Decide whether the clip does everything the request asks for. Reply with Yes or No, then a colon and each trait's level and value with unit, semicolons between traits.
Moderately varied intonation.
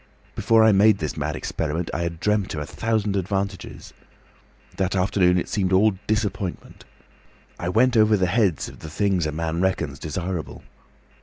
Yes: average, 3.5 semitones